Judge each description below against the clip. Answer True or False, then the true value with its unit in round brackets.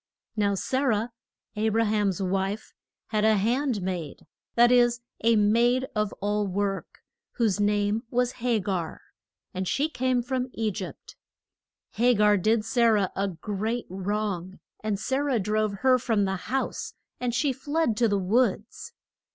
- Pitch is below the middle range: False (215 Hz)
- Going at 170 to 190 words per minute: False (160 wpm)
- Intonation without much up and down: False (3.3 semitones)